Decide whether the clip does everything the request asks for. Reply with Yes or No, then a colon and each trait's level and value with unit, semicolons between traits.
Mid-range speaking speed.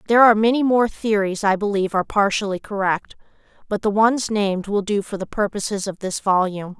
Yes: average, 195 wpm